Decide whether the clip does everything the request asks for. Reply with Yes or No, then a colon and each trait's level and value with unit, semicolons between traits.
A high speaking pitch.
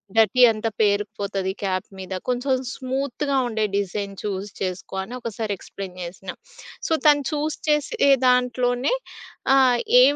Yes: high, 225 Hz